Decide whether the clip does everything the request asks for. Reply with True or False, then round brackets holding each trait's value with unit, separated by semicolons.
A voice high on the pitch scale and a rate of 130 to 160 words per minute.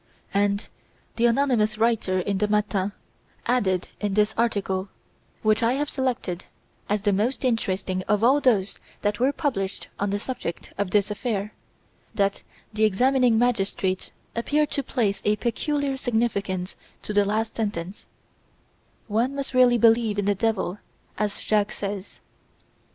True (210 Hz; 145 wpm)